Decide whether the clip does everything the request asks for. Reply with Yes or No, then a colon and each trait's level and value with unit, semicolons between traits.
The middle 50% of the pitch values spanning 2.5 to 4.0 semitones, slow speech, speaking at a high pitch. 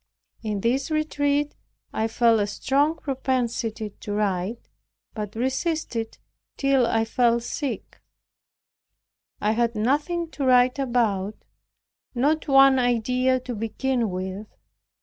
Yes: average, 3.6 semitones; slow, 115 wpm; high, 245 Hz